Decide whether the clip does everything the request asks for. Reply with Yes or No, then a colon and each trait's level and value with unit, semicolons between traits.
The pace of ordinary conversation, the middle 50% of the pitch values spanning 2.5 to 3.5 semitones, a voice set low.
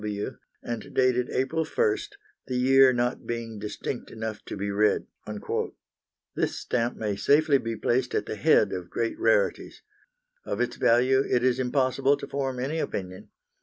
Yes: average, 165 wpm; average, 3.1 semitones; low, 125 Hz